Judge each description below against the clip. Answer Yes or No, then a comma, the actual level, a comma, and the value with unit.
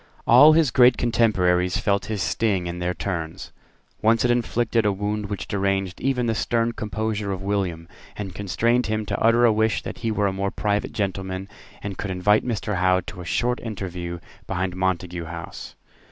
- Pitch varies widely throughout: No, average, 3.5 semitones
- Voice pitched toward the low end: Yes, low, 100 Hz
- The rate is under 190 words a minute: Yes, average, 180 wpm